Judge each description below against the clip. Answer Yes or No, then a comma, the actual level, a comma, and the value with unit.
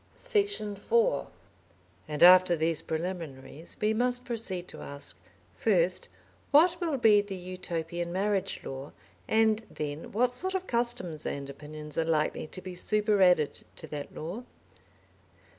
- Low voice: No, medium, 185 Hz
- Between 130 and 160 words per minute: Yes, slow, 135 wpm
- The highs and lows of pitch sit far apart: Yes, wide, 6.7 semitones